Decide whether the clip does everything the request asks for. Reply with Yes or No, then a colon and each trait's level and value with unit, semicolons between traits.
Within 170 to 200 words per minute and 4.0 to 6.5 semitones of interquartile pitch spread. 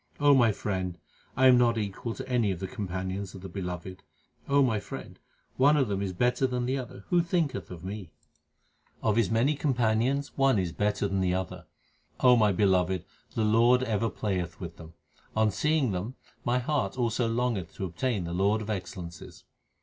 Yes: average, 185 wpm; average, 5.0 semitones